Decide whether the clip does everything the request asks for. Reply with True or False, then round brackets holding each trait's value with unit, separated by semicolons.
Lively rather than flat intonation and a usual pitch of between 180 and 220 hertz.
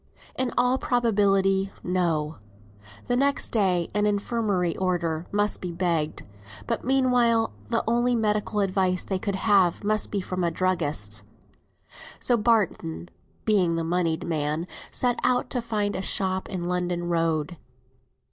False (4.1 semitones; 190 Hz)